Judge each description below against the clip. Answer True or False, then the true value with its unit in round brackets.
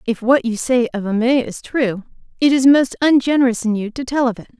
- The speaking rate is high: True (235 wpm)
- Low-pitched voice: False (245 Hz)